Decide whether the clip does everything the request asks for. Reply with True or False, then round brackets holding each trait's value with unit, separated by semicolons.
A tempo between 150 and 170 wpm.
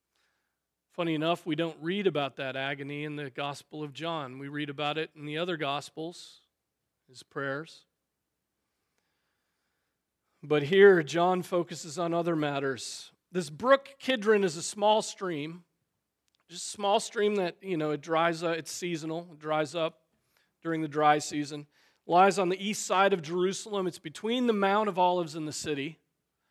True (165 wpm)